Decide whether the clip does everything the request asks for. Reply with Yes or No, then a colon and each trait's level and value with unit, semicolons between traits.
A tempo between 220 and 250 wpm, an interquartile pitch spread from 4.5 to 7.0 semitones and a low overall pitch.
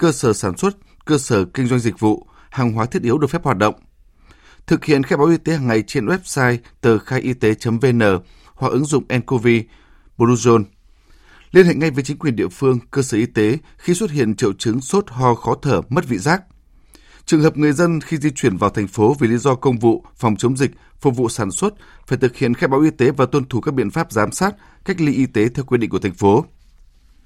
Yes: average, 240 wpm; average, 5.2 semitones; low, 125 Hz